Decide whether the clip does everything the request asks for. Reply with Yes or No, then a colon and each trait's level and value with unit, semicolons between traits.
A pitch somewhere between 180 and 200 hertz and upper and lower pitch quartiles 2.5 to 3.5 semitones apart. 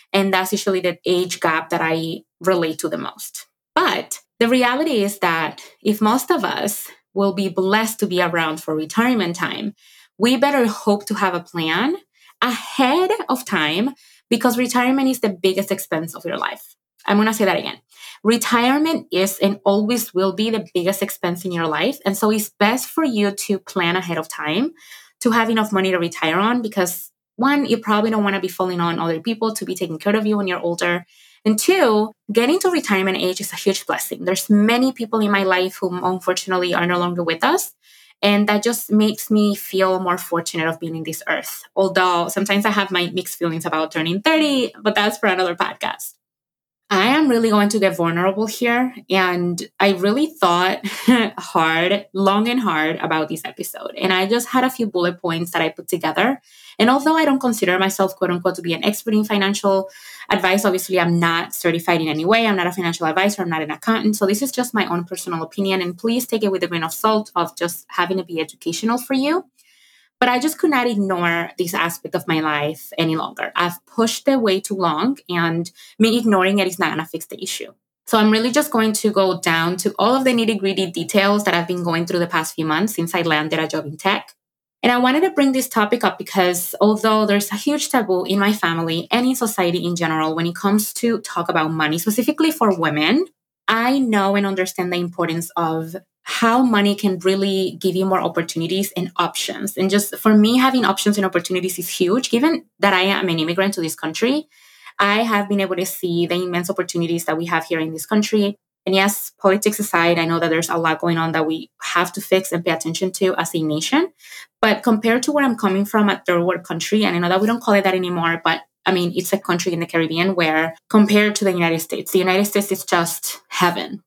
No: high, 190 Hz; average, 3.9 semitones